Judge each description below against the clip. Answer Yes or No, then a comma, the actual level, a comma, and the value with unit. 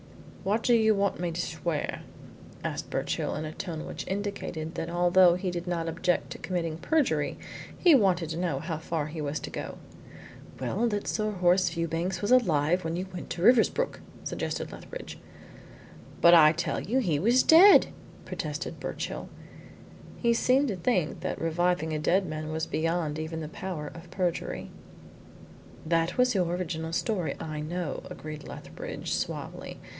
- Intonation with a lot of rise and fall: No, average, 3.6 semitones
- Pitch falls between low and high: Yes, medium, 175 Hz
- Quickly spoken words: No, average, 165 wpm